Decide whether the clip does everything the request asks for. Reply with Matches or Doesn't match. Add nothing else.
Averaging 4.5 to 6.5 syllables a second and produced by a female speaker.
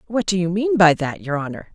Matches